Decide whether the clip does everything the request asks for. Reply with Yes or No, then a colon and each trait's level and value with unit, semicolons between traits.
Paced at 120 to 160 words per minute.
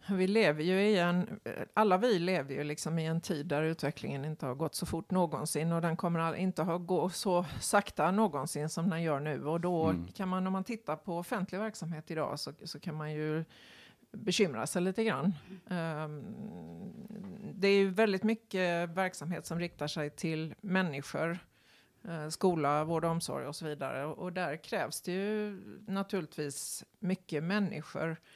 No: average, 170 wpm